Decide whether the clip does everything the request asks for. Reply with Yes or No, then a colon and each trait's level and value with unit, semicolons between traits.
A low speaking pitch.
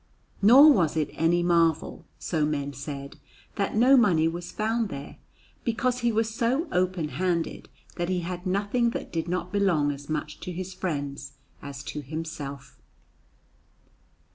No: medium, 175 Hz